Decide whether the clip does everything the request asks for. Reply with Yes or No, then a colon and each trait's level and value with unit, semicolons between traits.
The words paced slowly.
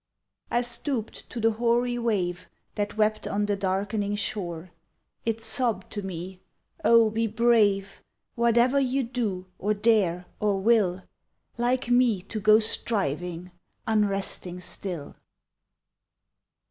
Yes: slow, 120 wpm